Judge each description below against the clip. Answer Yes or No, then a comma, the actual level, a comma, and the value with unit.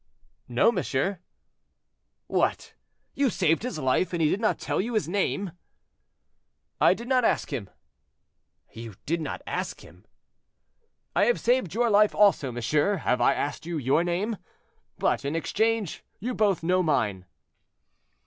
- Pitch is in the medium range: Yes, medium, 180 Hz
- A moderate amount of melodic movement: No, wide, 6.6 semitones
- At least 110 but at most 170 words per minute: Yes, average, 150 wpm